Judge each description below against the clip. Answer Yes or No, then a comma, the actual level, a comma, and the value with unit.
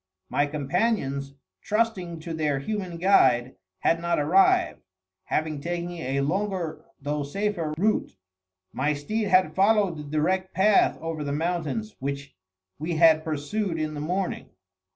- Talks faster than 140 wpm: No, slow, 135 wpm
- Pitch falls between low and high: Yes, medium, 165 Hz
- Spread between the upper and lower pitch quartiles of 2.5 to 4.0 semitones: No, average, 4.4 semitones